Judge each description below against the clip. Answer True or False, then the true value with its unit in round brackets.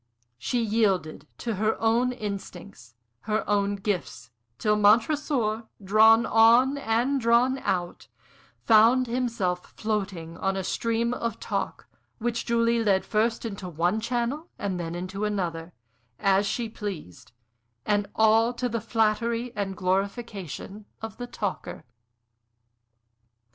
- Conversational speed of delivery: False (120 wpm)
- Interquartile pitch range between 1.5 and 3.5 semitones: True (3.2 semitones)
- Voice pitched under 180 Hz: False (215 Hz)